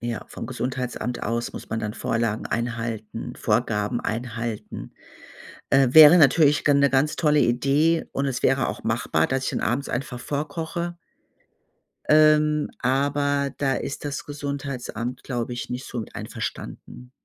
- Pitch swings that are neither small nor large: Yes, average, 3.4 semitones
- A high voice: No, low, 130 Hz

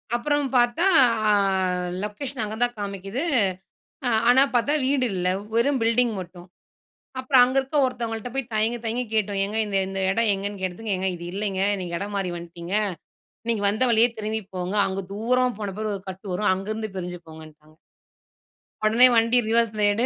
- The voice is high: Yes, high, 215 Hz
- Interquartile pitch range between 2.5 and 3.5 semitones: No, average, 3.9 semitones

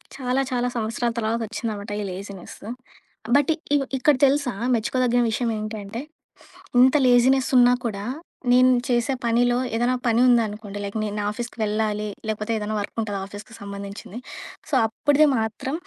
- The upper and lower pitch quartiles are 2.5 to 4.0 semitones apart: Yes, average, 2.8 semitones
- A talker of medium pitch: No, high, 230 Hz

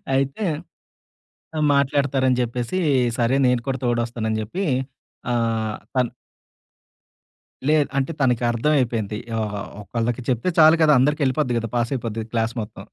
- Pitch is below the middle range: Yes, low, 120 Hz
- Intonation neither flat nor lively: Yes, average, 3.0 semitones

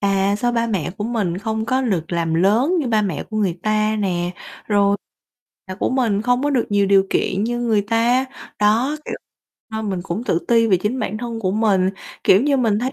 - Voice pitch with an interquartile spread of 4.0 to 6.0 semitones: No, average, 3.3 semitones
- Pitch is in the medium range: No, high, 215 Hz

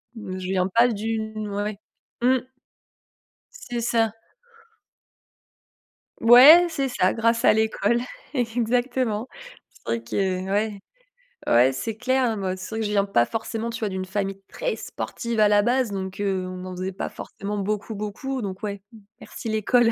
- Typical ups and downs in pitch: Yes, average, 3.4 semitones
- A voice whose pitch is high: Yes, high, 215 Hz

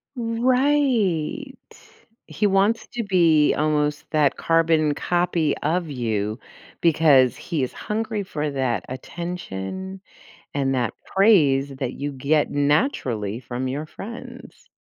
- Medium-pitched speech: Yes, medium, 155 Hz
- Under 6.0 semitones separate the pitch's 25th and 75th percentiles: No, wide, 6.3 semitones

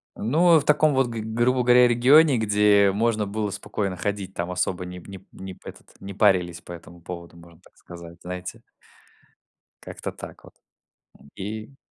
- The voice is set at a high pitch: No, low, 100 Hz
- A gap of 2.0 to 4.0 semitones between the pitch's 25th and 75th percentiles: No, average, 4.7 semitones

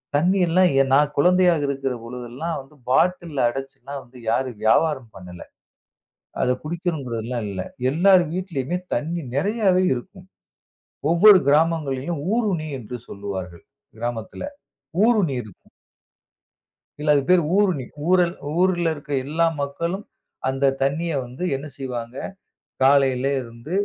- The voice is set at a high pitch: No, medium, 145 Hz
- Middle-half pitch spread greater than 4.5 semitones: Yes, wide, 5.5 semitones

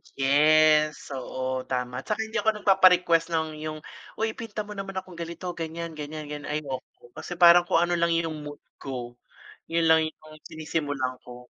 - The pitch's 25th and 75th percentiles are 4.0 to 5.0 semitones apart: No, average, 3.1 semitones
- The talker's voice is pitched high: No, medium, 155 Hz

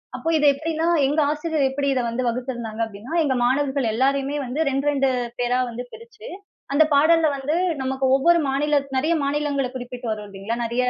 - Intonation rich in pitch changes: No, average, 3.2 semitones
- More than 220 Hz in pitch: Yes, very high, 275 Hz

